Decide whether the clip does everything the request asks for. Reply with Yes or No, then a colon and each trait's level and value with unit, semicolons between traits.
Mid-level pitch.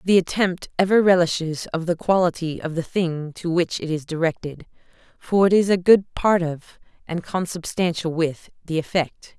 Yes: medium, 170 Hz